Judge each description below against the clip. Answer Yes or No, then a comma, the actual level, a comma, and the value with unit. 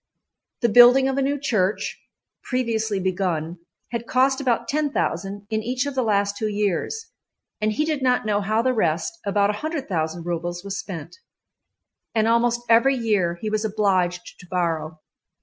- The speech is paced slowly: No, average, 160 wpm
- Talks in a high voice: Yes, high, 215 Hz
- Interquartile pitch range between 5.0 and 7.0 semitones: Yes, average, 5.3 semitones